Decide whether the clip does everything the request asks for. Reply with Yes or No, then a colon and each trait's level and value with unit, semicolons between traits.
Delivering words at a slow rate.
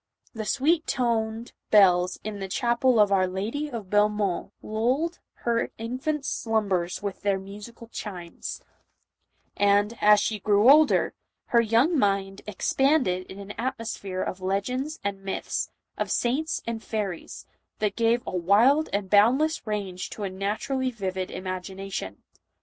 No: average, 145 wpm